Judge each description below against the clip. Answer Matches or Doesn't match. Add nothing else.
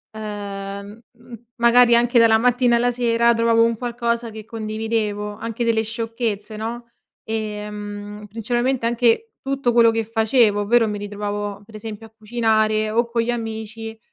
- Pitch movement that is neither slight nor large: Doesn't match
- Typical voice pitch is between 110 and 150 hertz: Doesn't match